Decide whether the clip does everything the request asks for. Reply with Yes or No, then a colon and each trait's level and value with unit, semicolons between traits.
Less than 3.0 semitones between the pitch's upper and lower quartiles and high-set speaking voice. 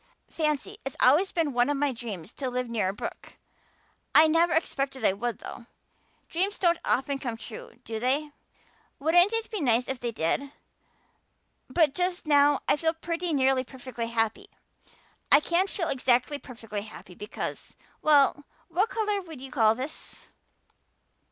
No: average, 5.3 semitones; very high, 275 Hz